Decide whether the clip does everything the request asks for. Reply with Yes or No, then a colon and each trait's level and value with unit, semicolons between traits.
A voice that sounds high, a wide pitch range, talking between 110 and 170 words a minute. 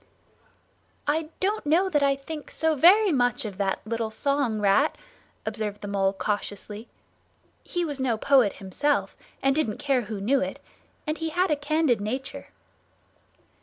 Yes: very high, 270 Hz; wide, 6.3 semitones; average, 155 wpm